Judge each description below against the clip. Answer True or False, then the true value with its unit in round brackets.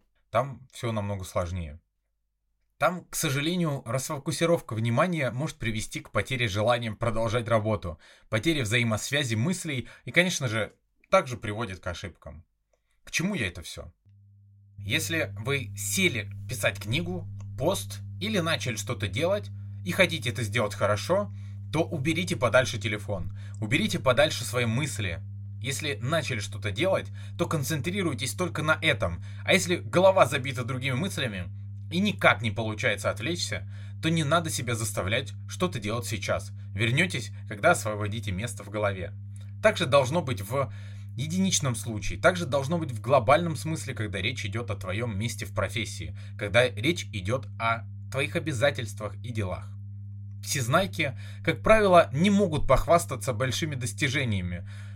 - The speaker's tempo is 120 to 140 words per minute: True (135 wpm)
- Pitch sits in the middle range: False (110 Hz)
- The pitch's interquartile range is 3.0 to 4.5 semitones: False (4.9 semitones)